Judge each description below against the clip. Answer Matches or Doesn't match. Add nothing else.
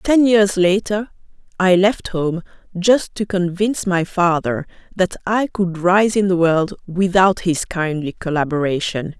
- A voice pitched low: Doesn't match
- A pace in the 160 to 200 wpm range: Doesn't match